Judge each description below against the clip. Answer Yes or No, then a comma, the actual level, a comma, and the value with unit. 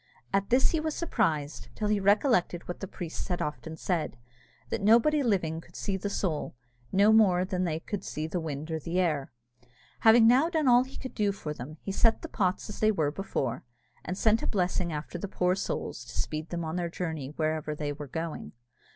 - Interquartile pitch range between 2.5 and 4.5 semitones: No, average, 5.0 semitones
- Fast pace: Yes, fast, 215 wpm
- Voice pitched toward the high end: No, medium, 180 Hz